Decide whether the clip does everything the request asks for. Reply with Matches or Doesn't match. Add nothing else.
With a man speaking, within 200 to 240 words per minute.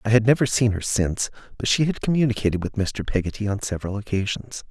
Matches